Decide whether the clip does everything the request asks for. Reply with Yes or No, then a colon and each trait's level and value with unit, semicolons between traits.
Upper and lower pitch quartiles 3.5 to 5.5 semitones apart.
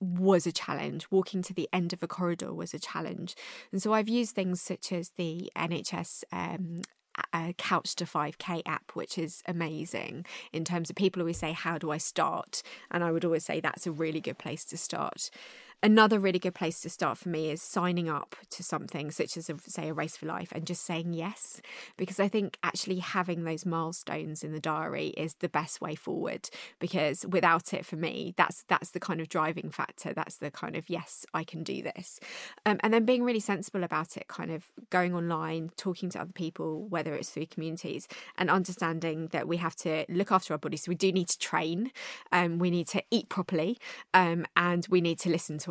No: narrow, 2.4 semitones